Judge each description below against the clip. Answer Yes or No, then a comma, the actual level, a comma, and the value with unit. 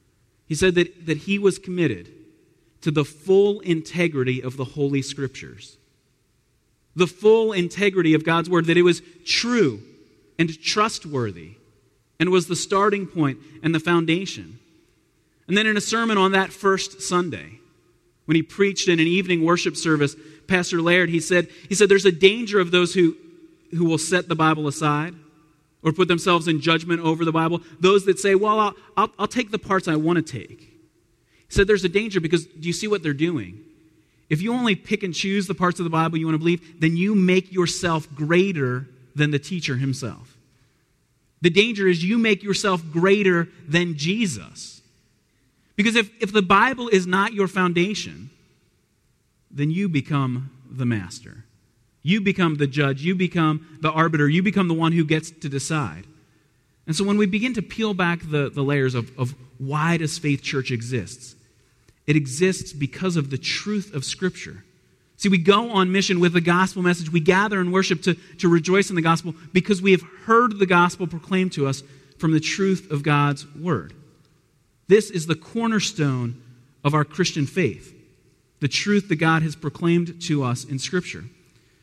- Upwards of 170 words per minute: Yes, average, 180 wpm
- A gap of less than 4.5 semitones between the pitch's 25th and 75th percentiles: No, average, 4.9 semitones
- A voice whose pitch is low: No, medium, 165 Hz